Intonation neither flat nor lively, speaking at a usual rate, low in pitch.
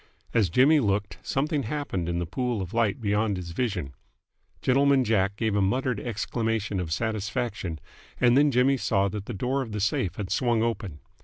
Yes: average, 4.4 semitones; average, 180 wpm; low, 110 Hz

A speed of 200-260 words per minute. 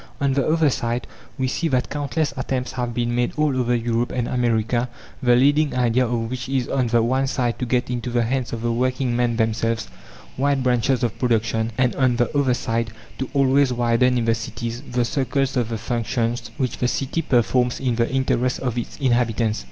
Yes: fast, 205 wpm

